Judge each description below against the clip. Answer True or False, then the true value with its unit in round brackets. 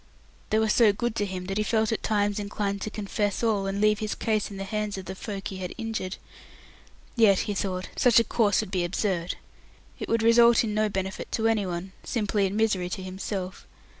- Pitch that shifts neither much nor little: False (2.3 semitones)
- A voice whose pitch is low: False (205 Hz)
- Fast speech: True (215 wpm)